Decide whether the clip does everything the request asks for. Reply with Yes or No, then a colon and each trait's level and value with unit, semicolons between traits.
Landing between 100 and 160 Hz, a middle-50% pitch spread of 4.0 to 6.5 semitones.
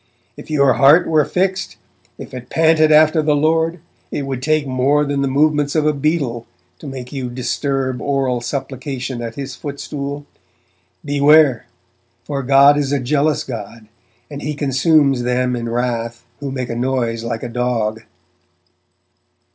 No: medium, 140 Hz; average, 3.1 semitones